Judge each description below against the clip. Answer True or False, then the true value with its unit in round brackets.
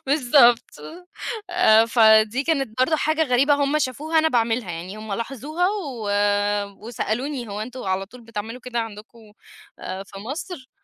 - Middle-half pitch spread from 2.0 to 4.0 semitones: False (4.7 semitones)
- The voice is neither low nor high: False (245 Hz)